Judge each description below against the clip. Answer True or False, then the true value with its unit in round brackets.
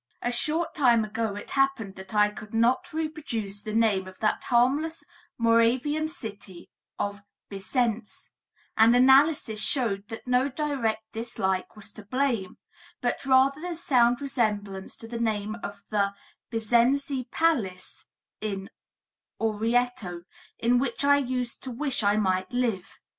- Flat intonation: False (4.2 semitones)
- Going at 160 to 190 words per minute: False (135 wpm)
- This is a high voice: True (230 Hz)